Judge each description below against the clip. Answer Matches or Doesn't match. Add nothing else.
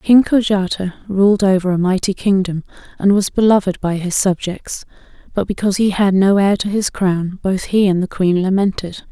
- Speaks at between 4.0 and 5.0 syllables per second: Matches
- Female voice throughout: Matches